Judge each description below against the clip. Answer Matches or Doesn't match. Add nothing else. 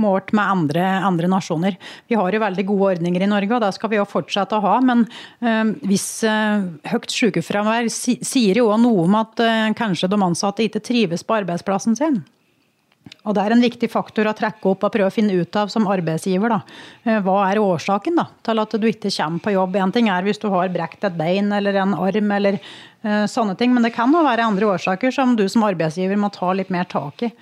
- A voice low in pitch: Doesn't match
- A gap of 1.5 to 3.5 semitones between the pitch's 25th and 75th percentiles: Matches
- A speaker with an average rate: Doesn't match